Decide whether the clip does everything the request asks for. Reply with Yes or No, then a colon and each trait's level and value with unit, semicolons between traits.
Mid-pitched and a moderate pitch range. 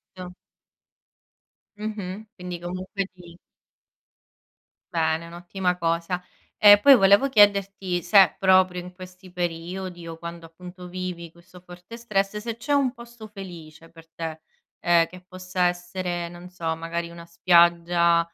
No: medium, 180 Hz; narrow, 2.2 semitones